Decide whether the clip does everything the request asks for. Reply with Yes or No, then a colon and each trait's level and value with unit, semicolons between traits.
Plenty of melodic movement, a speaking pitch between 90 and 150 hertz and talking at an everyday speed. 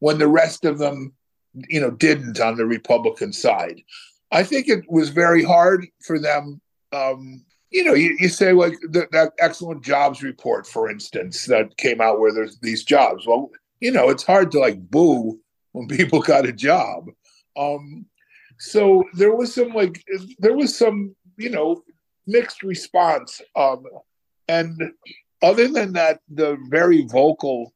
No: wide, 5.8 semitones; medium, 165 Hz; average, 160 wpm